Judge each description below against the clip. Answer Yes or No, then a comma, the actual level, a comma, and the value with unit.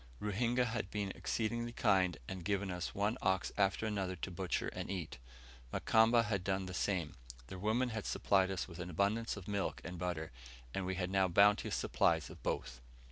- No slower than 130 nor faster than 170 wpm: No, average, 190 wpm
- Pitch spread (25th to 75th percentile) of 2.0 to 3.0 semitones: Yes, narrow, 2.6 semitones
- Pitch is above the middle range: No, very low, 95 Hz